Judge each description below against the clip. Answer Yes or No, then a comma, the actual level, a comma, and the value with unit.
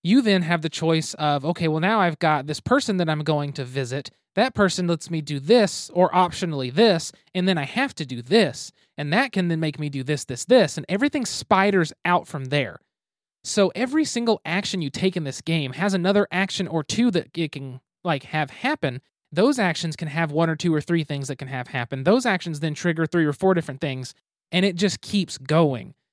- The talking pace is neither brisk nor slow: No, fast, 225 wpm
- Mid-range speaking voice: Yes, medium, 165 Hz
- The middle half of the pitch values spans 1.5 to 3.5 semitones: No, average, 4.3 semitones